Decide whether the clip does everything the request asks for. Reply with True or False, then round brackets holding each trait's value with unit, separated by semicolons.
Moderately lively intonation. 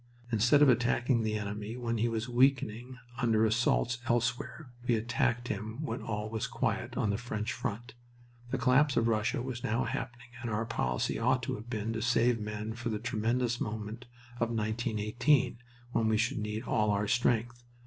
False (2.1 semitones)